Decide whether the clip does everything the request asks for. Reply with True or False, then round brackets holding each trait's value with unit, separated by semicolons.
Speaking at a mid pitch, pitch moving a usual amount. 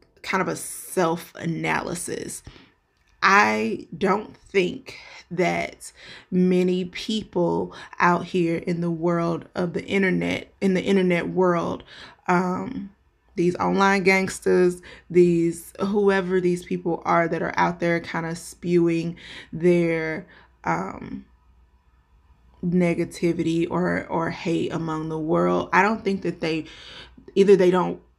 False (170 Hz; 1.9 semitones)